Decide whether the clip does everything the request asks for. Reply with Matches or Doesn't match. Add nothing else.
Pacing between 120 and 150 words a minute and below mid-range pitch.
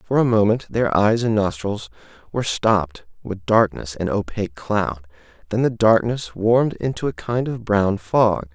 Doesn't match